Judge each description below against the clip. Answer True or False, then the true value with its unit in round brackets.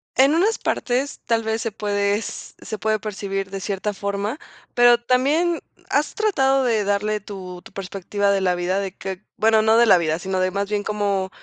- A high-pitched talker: True (205 Hz)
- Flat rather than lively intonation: False (3.3 semitones)